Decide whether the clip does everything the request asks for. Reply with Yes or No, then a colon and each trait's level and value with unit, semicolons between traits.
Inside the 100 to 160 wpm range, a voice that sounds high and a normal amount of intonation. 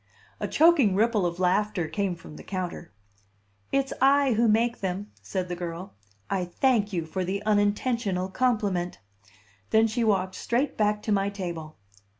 Yes: average, 155 wpm; high, 200 Hz; average, 3.8 semitones